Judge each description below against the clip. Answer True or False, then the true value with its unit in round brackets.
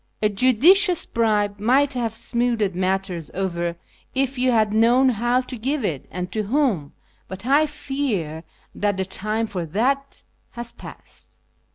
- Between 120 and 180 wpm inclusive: True (150 wpm)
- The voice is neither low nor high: False (225 Hz)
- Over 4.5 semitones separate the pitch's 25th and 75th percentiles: True (5.1 semitones)